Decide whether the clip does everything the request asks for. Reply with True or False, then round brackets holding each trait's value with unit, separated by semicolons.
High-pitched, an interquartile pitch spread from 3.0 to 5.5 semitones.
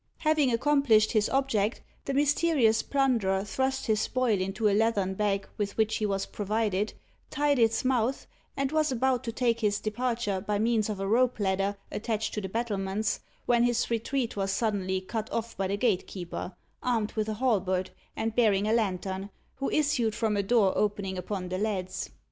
True (220 Hz; 3.4 semitones)